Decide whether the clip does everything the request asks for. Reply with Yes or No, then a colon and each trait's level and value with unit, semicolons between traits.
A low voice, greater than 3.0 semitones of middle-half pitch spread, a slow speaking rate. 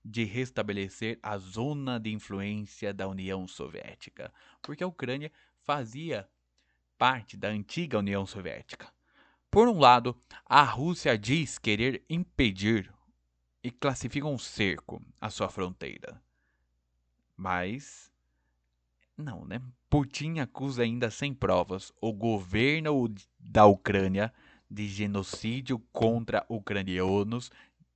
Yes: low, 110 Hz; average, 5.2 semitones; slow, 105 wpm